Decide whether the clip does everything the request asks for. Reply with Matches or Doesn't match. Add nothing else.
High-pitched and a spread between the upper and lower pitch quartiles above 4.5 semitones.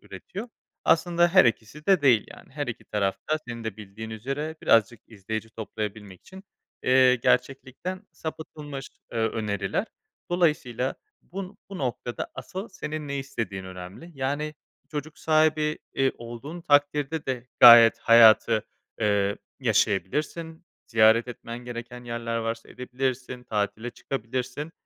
Doesn't match